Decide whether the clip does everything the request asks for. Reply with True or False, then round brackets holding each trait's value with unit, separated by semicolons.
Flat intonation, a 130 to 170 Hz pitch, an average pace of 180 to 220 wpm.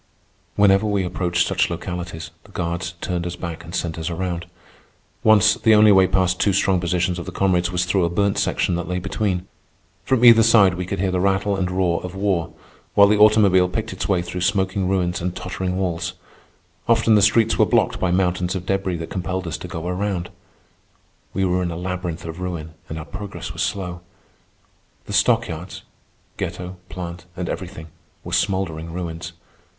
False (1.9 semitones; 90 Hz; 185 wpm)